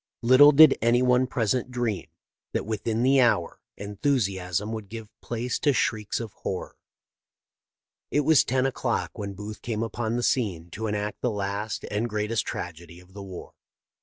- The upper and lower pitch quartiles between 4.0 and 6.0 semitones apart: No, average, 3.4 semitones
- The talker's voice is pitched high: No, low, 110 Hz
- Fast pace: No, average, 160 wpm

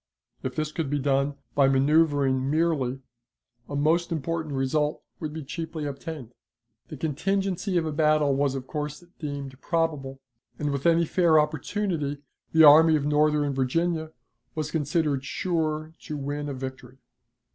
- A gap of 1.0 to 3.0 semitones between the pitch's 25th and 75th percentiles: Yes, narrow, 2.6 semitones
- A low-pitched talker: No, medium, 150 Hz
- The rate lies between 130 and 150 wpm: Yes, average, 145 wpm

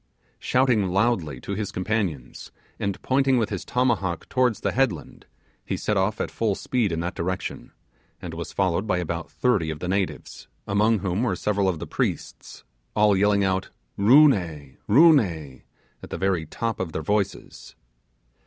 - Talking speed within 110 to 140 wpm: No, average, 170 wpm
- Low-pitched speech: Yes, low, 100 Hz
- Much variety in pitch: No, average, 4.3 semitones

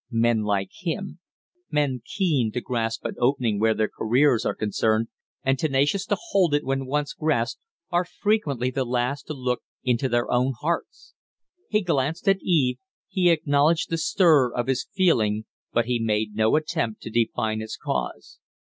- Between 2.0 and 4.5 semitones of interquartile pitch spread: No, wide, 5.5 semitones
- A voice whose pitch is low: Yes, low, 130 Hz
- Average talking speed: Yes, average, 170 wpm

